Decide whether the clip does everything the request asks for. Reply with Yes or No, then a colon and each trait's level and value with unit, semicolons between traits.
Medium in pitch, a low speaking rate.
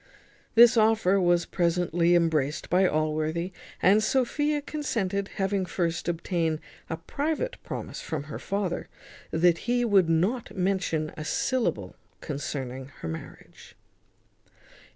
Yes: medium, 175 Hz; slow, 115 wpm